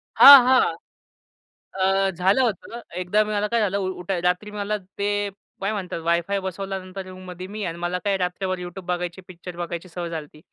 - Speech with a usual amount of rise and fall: No, narrow, 2.3 semitones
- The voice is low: No, medium, 185 Hz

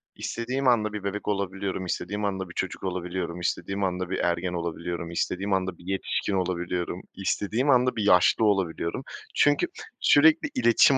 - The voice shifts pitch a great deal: No, average, 3.0 semitones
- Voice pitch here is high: No, very low, 95 Hz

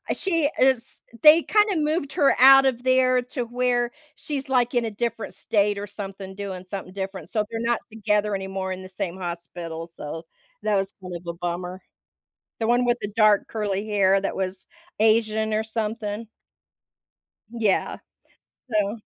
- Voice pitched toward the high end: Yes, high, 215 Hz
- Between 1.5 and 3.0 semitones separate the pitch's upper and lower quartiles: No, average, 4.0 semitones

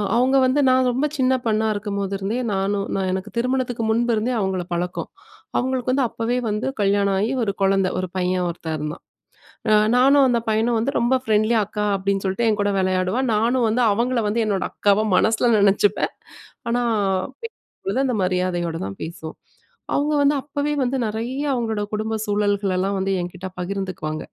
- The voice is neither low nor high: No, high, 215 Hz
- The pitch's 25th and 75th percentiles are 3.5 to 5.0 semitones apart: Yes, average, 4.2 semitones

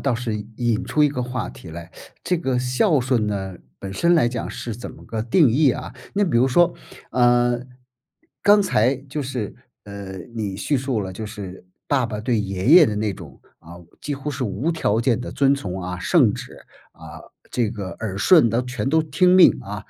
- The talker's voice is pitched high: No, low, 120 Hz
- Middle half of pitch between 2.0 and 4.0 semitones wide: No, average, 5.3 semitones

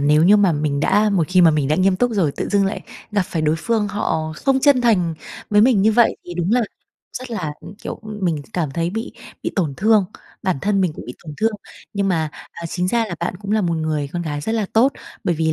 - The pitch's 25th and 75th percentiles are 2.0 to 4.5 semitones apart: No, average, 5.1 semitones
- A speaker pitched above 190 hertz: No, medium, 185 Hz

